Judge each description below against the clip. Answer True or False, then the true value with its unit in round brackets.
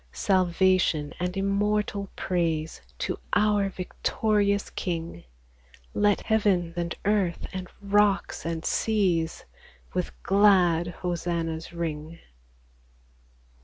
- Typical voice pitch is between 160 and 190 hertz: True (185 Hz)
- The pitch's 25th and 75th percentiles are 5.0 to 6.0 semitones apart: False (3.1 semitones)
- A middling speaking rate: False (90 wpm)